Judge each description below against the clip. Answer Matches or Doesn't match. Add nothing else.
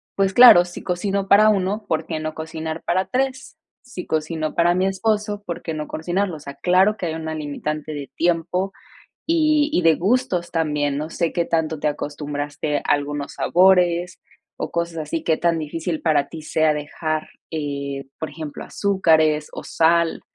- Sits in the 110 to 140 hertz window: Doesn't match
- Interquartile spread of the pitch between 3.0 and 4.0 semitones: Matches